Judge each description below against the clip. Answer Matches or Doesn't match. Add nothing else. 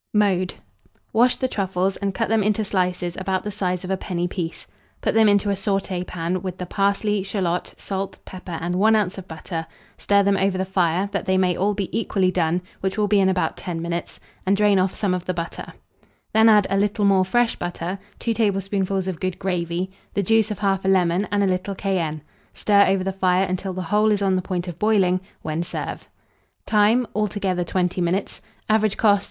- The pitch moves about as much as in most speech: Doesn't match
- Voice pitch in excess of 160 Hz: Matches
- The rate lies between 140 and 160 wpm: Doesn't match